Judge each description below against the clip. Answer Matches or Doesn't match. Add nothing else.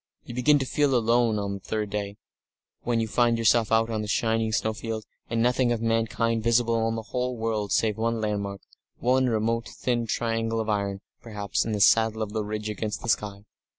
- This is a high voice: Doesn't match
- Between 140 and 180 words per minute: Doesn't match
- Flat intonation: Matches